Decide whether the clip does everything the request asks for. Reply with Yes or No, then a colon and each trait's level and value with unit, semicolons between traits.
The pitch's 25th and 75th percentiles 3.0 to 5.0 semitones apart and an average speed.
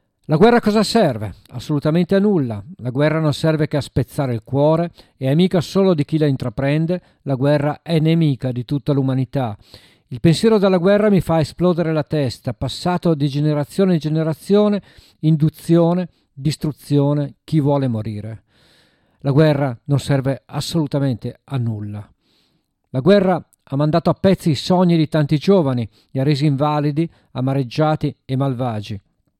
Yes: average, 4.0 semitones; average, 155 wpm